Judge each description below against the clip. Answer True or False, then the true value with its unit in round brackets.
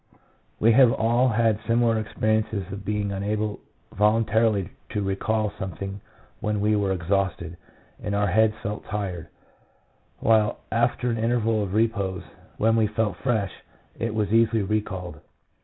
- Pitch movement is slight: True (2.1 semitones)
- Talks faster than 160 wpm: False (140 wpm)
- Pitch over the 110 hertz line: False (105 Hz)